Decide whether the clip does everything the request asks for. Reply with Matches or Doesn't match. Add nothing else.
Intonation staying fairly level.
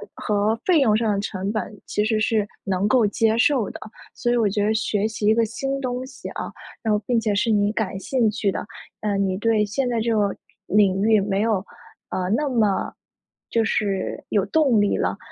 Matches